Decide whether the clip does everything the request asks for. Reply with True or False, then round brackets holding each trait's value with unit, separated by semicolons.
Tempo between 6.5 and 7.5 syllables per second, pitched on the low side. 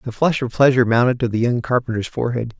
True (6.9 syllables/s; 120 Hz)